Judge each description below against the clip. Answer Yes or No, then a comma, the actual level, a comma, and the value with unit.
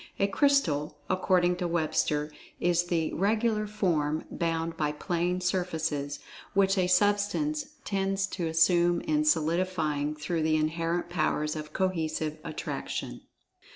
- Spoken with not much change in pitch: No, average, 3.7 semitones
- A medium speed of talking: No, slow, 125 wpm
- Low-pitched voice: No, medium, 175 Hz